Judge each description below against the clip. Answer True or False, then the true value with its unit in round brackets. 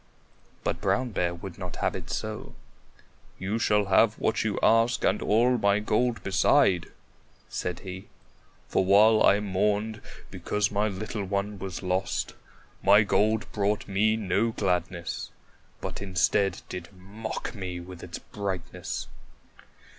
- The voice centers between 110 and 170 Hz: False (100 Hz)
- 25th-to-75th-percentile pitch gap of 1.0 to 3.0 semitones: True (2.6 semitones)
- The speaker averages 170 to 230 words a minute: False (135 wpm)